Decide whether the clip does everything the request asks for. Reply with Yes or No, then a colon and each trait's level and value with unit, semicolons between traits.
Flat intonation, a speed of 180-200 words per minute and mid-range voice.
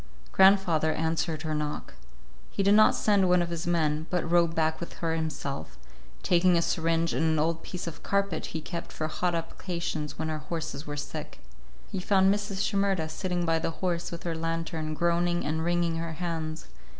Yes: narrow, 1.9 semitones; average, 185 wpm; medium, 165 Hz